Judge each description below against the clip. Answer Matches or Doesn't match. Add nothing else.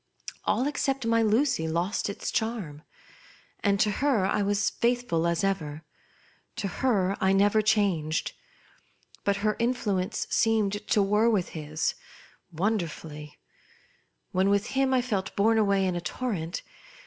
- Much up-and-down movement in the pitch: Doesn't match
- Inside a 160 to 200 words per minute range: Doesn't match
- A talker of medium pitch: Doesn't match